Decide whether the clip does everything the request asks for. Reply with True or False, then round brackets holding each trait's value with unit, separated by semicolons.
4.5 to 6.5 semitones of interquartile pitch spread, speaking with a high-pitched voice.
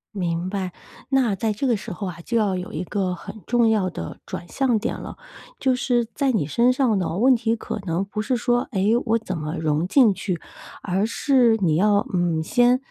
True (5.0 semitones; 210 Hz)